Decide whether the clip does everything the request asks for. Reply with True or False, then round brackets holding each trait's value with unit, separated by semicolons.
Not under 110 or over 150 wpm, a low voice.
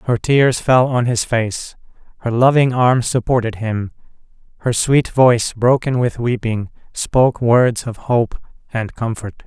True (145 wpm; 120 Hz)